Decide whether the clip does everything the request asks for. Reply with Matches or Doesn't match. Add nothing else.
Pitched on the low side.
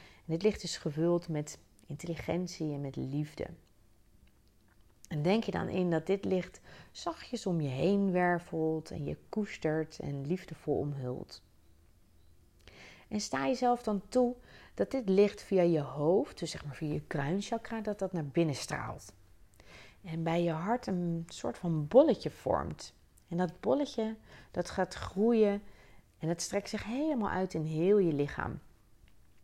Doesn't match